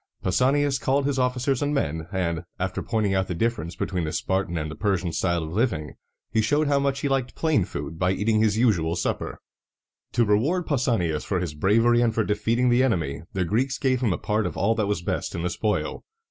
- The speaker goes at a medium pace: No, fast, 215 wpm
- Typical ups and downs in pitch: No, wide, 6.2 semitones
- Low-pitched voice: Yes, low, 105 Hz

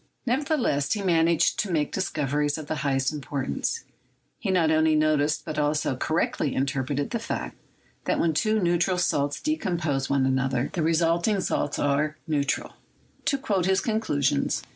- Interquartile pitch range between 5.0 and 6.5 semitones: No, average, 4.3 semitones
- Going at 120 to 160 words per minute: No, average, 170 wpm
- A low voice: No, medium, 155 Hz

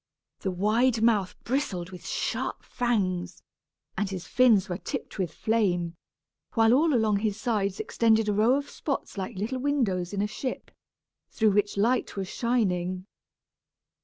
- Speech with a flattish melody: No, average, 4.1 semitones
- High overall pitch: Yes, high, 210 Hz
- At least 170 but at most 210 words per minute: No, average, 150 wpm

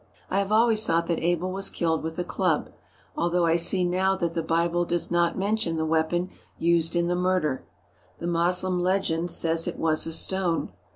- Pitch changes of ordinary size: No, narrow, 2.0 semitones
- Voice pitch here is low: No, medium, 175 Hz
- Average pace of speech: Yes, average, 195 wpm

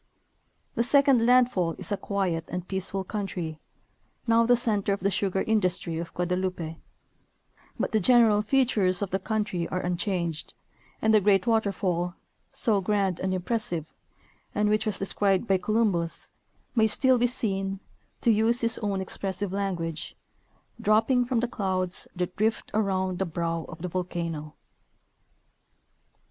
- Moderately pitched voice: No, high, 195 Hz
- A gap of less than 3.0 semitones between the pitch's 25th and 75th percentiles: No, average, 3.5 semitones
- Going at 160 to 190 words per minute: No, average, 145 wpm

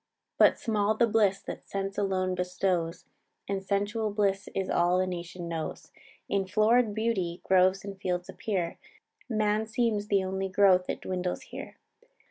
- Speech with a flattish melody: Yes, narrow, 2.3 semitones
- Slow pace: No, average, 150 wpm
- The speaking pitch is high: Yes, high, 195 Hz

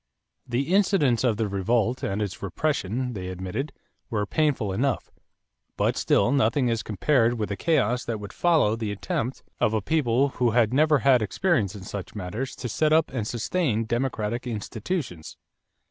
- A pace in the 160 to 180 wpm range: Yes, average, 165 wpm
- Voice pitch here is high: No, low, 120 Hz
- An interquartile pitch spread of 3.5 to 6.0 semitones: Yes, average, 4.6 semitones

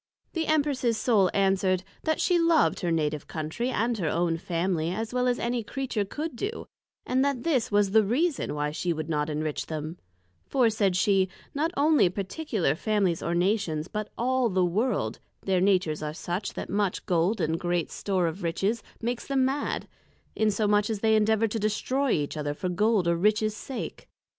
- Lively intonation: Yes, wide, 5.8 semitones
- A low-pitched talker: No, high, 205 Hz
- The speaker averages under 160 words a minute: No, average, 180 wpm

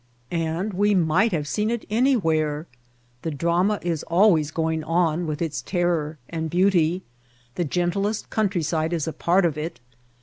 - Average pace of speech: Yes, average, 155 wpm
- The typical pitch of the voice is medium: Yes, medium, 170 Hz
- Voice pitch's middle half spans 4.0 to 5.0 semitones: No, average, 3.2 semitones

